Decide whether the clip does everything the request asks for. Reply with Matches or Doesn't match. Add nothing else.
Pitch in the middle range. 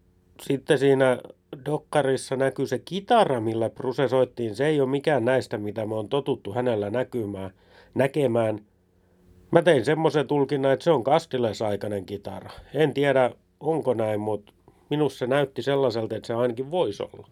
Doesn't match